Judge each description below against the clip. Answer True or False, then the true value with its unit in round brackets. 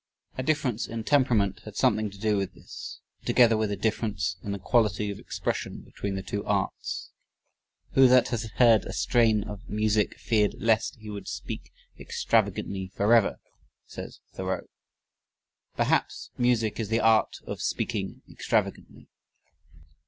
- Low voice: True (110 Hz)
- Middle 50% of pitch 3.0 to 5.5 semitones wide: False (2.4 semitones)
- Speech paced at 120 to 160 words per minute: True (145 wpm)